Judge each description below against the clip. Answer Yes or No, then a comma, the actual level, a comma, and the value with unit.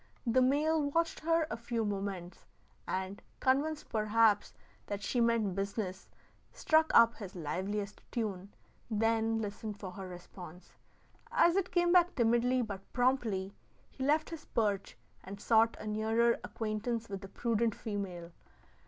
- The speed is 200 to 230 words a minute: No, average, 140 wpm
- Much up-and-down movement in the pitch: No, average, 3.8 semitones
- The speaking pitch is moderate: No, high, 220 Hz